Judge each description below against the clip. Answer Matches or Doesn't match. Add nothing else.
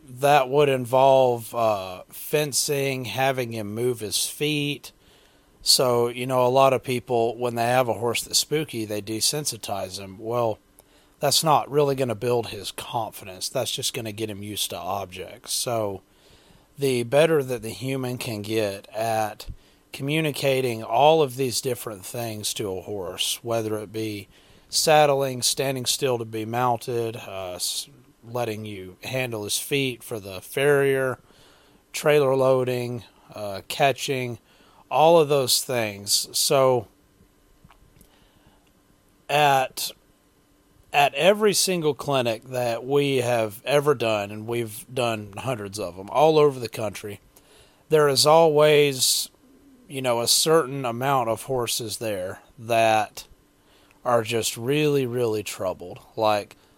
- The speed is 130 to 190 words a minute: Matches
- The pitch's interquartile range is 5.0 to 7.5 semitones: Doesn't match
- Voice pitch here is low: Matches